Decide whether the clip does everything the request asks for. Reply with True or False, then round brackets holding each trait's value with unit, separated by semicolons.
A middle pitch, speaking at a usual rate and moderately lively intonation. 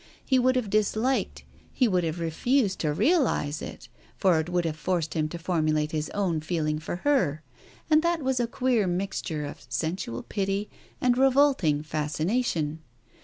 False (180 Hz; 170 wpm; 8.0 semitones)